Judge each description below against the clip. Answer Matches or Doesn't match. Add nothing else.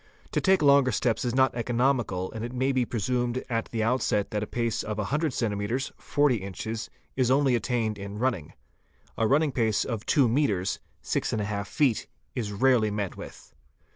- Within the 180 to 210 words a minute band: Matches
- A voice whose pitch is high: Doesn't match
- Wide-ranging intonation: Doesn't match